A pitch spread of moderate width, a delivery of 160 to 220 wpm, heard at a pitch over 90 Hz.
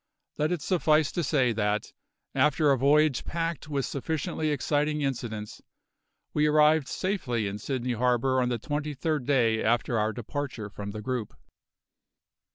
No: average, 4.4 semitones; average, 150 wpm; low, 135 Hz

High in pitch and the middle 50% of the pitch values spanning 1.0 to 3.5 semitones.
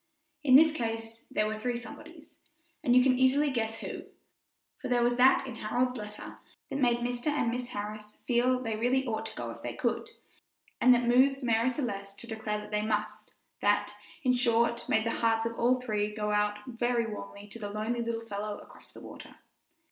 Yes: high, 230 Hz; average, 2.8 semitones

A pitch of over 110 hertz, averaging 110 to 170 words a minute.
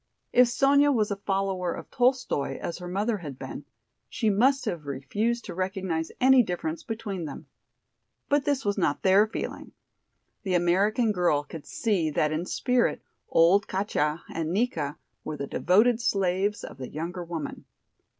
Yes: high, 190 Hz; average, 160 wpm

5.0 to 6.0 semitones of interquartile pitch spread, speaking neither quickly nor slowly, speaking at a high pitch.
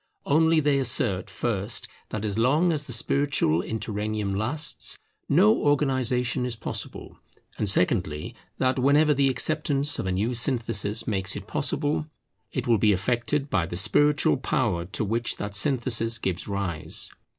No: wide, 5.4 semitones; average, 150 wpm; low, 115 Hz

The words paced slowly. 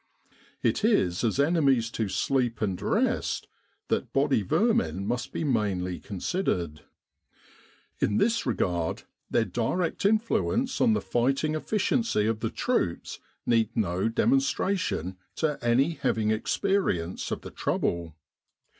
Yes: slow, 130 wpm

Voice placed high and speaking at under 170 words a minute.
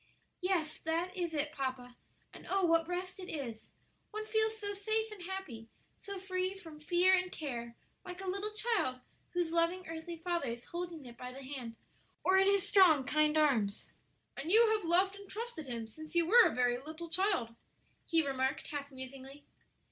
No: very high, 335 Hz; average, 185 wpm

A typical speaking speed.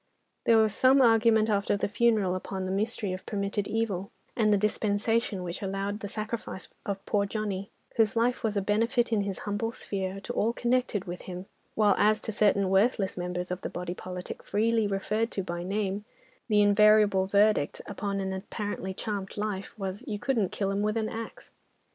Yes: average, 185 wpm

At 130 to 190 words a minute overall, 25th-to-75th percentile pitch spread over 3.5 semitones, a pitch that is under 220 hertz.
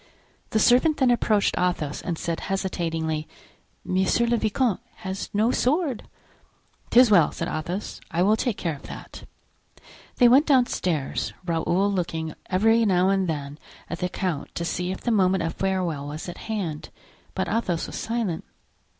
Yes: average, 160 wpm; average, 5.1 semitones; high, 190 Hz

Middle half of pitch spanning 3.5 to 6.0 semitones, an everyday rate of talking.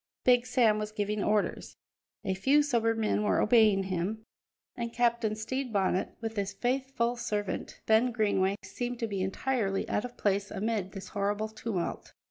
No: average, 3.0 semitones; average, 160 wpm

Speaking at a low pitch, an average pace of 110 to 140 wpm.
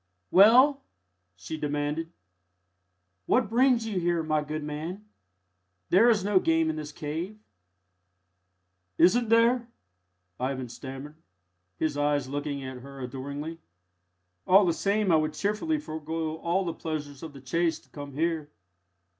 No: medium, 160 Hz; slow, 135 wpm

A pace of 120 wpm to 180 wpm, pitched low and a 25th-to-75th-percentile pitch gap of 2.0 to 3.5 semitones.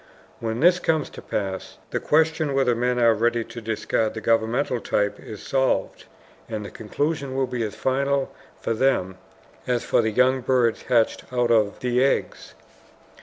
Yes: average, 170 wpm; low, 120 Hz; average, 3.1 semitones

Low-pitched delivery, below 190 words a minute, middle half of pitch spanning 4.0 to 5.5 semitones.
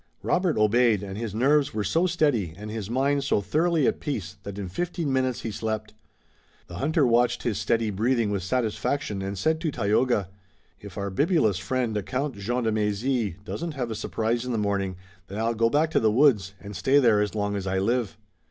No: low, 115 Hz; fast, 205 wpm; average, 4.5 semitones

